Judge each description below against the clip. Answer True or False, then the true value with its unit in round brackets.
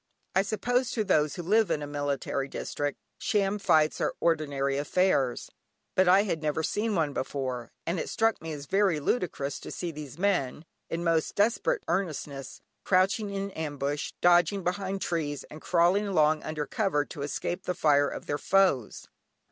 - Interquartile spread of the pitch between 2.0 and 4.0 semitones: False (5.1 semitones)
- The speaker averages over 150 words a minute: True (170 wpm)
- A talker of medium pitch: True (165 Hz)